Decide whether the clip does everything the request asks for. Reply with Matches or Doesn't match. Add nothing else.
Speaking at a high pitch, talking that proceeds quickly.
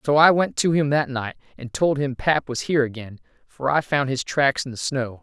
Doesn't match